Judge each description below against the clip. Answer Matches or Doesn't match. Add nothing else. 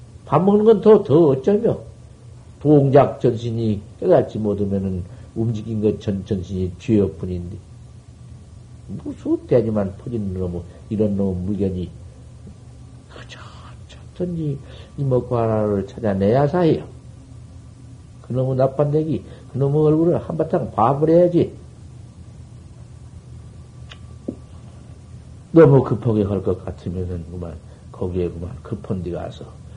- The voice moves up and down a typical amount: Matches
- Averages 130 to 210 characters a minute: Doesn't match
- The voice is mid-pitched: Doesn't match